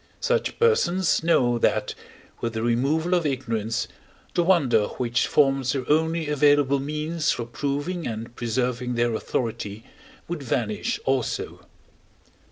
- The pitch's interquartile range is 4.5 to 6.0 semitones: Yes, average, 5.1 semitones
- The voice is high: No, low, 135 Hz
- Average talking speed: No, slow, 125 wpm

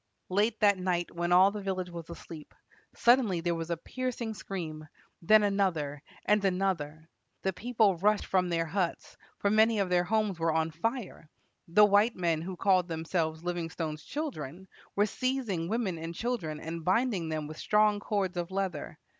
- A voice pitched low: No, medium, 185 Hz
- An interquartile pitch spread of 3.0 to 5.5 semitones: Yes, average, 4.1 semitones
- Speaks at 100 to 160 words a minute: No, average, 170 wpm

